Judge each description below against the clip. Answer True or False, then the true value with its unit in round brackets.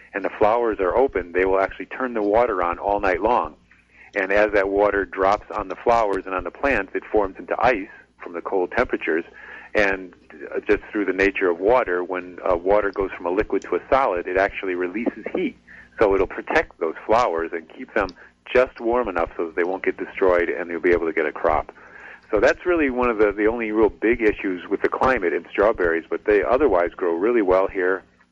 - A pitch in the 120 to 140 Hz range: False (110 Hz)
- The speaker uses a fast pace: True (225 wpm)